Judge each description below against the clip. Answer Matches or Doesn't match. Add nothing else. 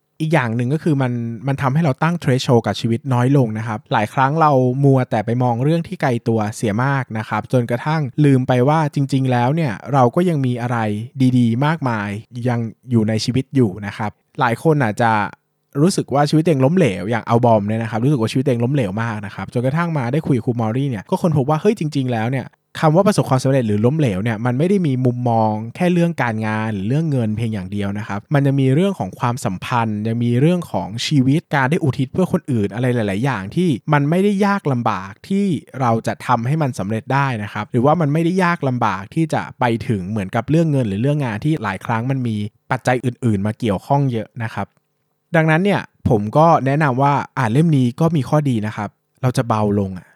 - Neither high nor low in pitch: Doesn't match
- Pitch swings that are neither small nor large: Matches